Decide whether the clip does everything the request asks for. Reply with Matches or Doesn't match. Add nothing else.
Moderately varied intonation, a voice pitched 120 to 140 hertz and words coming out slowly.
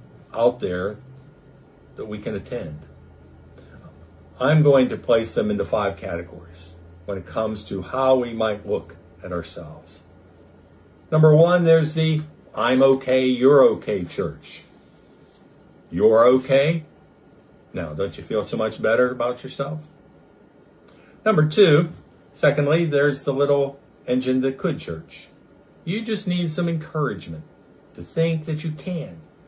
Doesn't match